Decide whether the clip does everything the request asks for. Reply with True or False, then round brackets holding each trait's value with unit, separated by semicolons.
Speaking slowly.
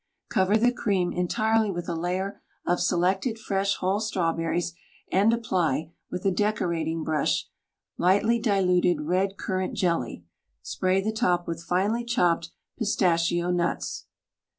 True (130 wpm)